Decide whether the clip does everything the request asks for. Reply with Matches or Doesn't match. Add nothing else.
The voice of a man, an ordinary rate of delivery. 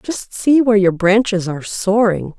Doesn't match